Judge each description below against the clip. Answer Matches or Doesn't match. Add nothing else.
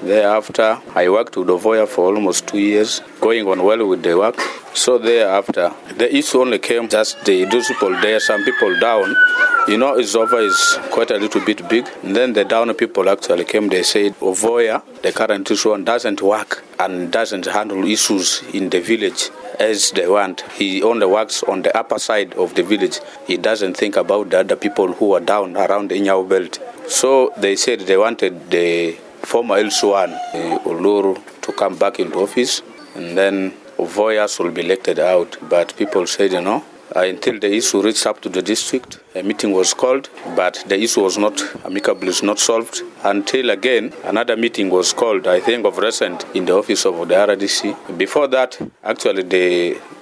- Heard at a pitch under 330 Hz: Doesn't match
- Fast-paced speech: Doesn't match